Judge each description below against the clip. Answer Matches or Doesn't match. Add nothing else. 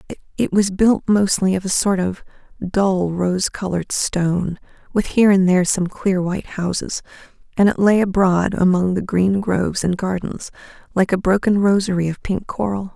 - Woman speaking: Matches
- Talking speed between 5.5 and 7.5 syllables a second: Doesn't match